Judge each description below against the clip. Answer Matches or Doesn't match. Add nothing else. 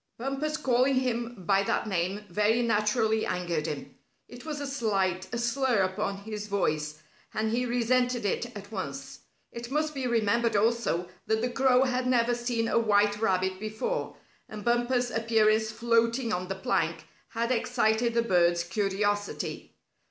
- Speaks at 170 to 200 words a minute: Doesn't match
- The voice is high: Matches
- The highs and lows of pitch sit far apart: Doesn't match